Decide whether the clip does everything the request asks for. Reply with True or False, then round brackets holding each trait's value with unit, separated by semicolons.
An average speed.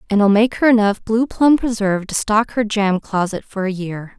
False (230 wpm)